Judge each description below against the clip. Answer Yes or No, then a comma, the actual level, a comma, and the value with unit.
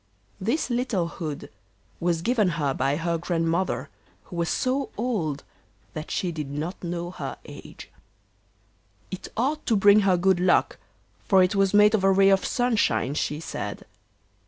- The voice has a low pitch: No, medium, 185 Hz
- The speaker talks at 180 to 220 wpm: No, average, 160 wpm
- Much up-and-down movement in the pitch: No, average, 3.9 semitones